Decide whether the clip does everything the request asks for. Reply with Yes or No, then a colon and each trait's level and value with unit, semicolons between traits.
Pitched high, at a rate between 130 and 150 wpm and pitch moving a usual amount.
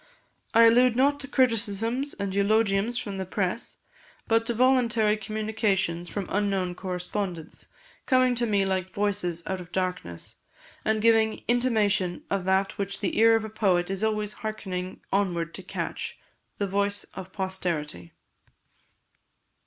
Yes: high, 205 Hz; average, 140 wpm; average, 3.2 semitones